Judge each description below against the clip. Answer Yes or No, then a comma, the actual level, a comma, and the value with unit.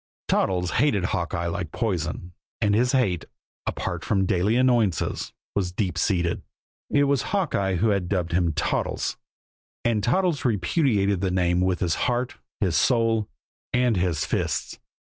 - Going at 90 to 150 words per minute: Yes, average, 145 wpm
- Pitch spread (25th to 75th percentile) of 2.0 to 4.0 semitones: No, average, 5.2 semitones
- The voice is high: No, low, 100 Hz